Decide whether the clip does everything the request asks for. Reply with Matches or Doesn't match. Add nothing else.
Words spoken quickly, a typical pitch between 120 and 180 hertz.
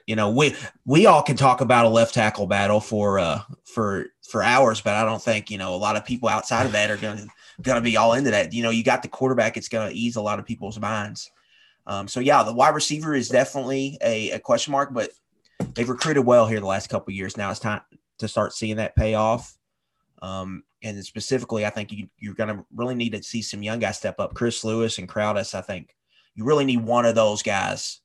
Doesn't match